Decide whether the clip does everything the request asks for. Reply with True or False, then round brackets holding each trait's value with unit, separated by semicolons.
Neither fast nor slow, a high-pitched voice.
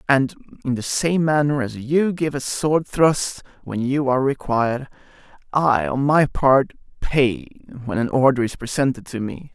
False (170 wpm; 135 Hz)